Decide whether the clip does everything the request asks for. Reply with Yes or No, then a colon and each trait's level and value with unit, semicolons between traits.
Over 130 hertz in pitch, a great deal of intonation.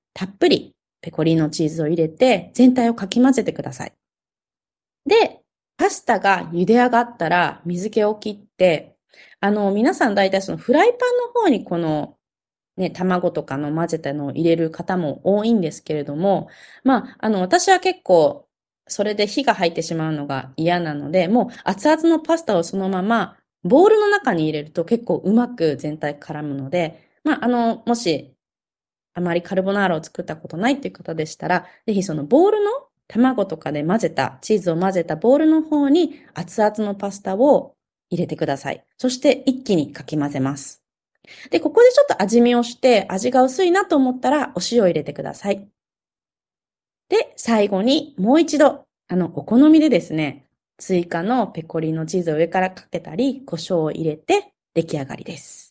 Yes: high, 190 Hz; wide, 7.5 semitones